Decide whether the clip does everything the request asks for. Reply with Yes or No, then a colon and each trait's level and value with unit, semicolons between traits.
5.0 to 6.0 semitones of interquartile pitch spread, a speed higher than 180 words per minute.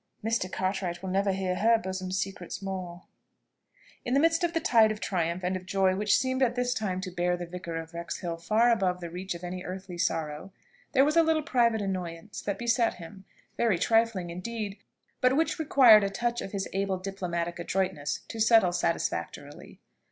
No: average, 4.3 semitones; average, 190 wpm